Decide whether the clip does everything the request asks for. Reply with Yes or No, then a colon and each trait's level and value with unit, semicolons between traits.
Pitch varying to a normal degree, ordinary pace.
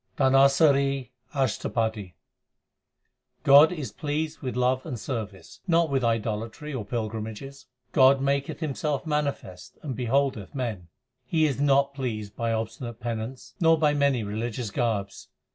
No: average, 3.9 semitones; slow, 125 wpm